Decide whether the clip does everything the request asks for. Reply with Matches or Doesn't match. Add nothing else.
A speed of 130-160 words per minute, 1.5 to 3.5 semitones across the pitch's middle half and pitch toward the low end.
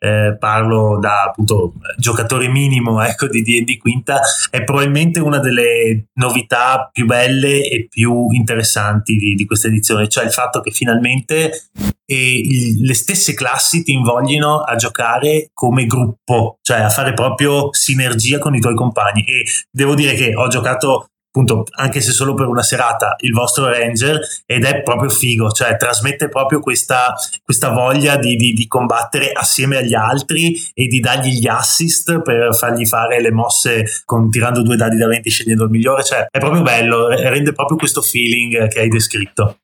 Doesn't match